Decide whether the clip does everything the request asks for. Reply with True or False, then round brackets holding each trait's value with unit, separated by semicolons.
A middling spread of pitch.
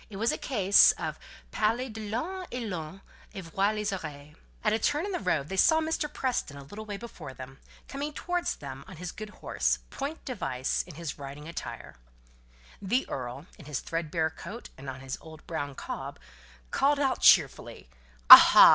False (8.7 semitones)